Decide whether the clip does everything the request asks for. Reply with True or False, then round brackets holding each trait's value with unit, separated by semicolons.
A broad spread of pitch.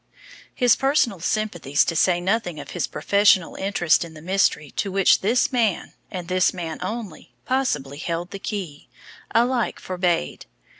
False (4.3 semitones)